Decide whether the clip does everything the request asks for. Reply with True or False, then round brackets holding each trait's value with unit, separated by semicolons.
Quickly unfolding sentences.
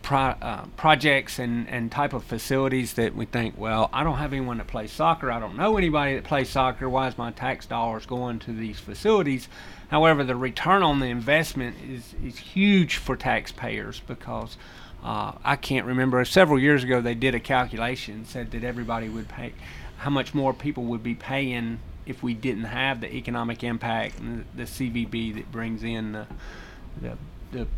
False (185 wpm)